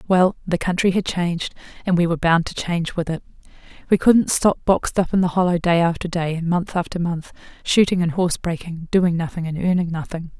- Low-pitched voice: No, medium, 175 Hz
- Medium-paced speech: No, fast, 215 wpm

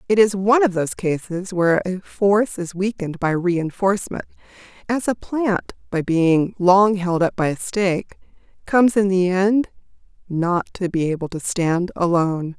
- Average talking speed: Yes, average, 160 wpm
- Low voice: No, medium, 185 Hz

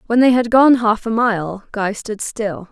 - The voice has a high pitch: Yes, high, 220 Hz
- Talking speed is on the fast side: Yes, fast, 220 wpm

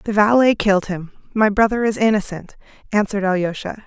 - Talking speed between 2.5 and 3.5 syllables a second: No, 5.8 syllables/s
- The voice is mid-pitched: No, high, 205 Hz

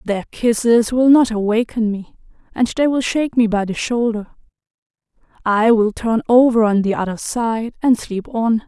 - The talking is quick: No, average, 175 wpm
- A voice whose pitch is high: Yes, high, 230 Hz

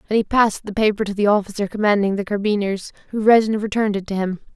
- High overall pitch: Yes, high, 205 Hz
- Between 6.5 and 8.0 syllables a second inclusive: Yes, 6.9 syllables/s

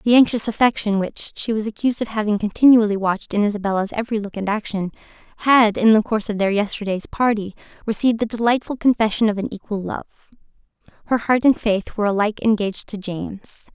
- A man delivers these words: No, female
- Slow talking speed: No, average, 185 wpm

